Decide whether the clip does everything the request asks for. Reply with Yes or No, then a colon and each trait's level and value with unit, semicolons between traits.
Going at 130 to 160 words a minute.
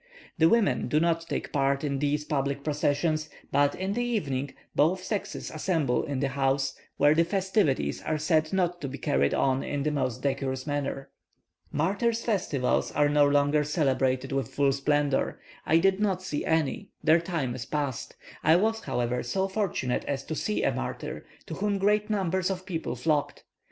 No: average, 175 wpm